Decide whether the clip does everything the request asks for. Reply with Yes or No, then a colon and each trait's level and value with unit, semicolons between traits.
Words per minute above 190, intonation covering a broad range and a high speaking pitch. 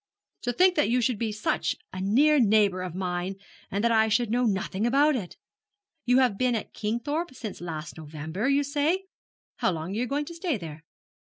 Yes: average, 200 wpm; wide, 6.3 semitones; high, 225 Hz